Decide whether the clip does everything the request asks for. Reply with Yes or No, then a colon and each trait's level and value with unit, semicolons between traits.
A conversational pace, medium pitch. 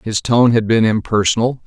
No: average, 180 wpm; low, 115 Hz